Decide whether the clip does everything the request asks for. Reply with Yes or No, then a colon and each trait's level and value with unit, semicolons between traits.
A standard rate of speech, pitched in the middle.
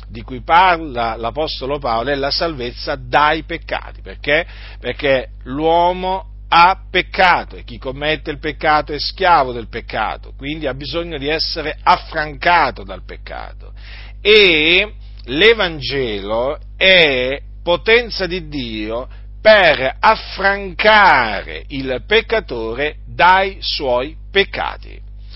No: slow, 105 wpm; medium, 145 Hz